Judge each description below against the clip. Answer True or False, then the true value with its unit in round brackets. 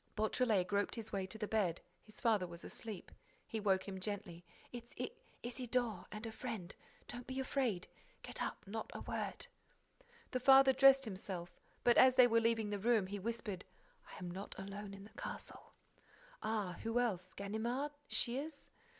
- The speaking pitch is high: True (220 Hz)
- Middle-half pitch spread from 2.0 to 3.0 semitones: False (3.7 semitones)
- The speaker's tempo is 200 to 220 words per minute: False (155 wpm)